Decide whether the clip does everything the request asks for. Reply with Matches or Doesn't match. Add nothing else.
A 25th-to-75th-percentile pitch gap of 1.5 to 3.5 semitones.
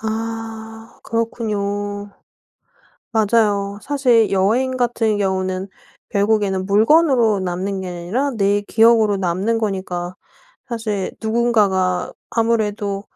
Matches